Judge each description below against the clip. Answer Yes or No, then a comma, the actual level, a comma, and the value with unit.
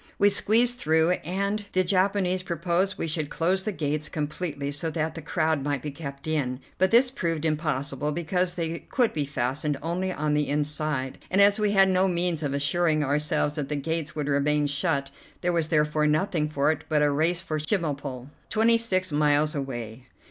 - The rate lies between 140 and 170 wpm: No, average, 185 wpm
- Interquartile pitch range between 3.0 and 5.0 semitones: Yes, average, 3.6 semitones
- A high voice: No, medium, 155 Hz